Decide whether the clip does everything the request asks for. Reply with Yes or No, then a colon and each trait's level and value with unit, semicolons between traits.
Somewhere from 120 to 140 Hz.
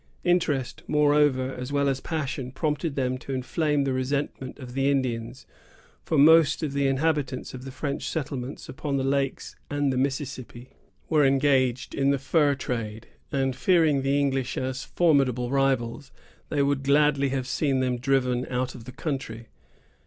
Yes: low, 135 Hz